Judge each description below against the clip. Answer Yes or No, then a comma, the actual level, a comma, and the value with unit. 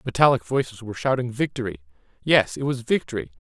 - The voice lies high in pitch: No, low, 120 Hz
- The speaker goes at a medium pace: Yes, average, 155 wpm